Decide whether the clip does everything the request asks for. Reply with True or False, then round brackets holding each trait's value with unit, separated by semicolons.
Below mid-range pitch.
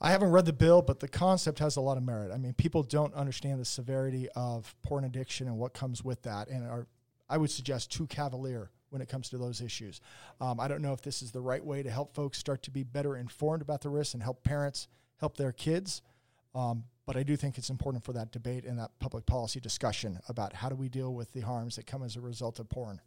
True (130 Hz)